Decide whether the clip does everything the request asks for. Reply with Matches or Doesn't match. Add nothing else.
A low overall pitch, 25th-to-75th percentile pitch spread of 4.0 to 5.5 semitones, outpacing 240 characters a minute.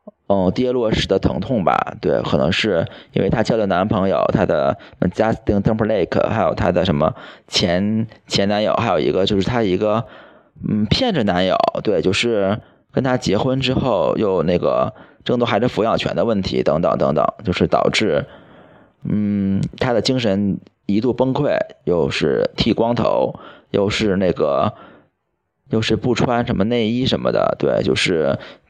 Doesn't match